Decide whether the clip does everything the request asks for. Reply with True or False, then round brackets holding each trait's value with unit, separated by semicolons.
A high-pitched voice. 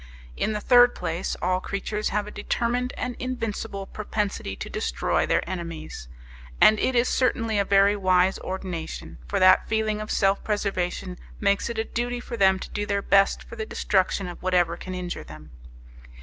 True (200 Hz)